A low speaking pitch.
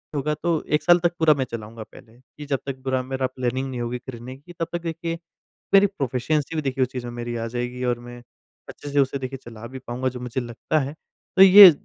Yes: low, 130 Hz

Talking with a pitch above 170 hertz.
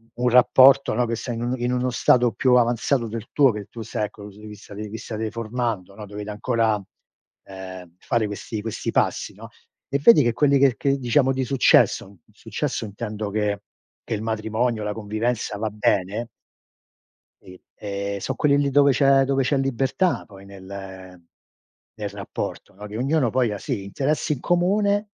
No: low, 115 Hz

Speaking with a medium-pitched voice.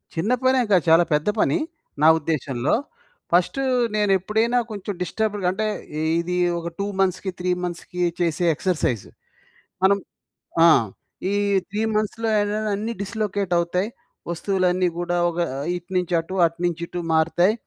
Yes: medium, 180 Hz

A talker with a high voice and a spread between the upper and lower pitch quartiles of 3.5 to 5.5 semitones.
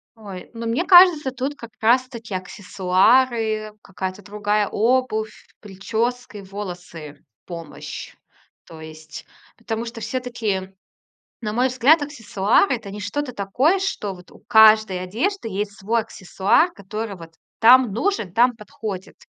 Yes: high, 215 Hz; average, 4.2 semitones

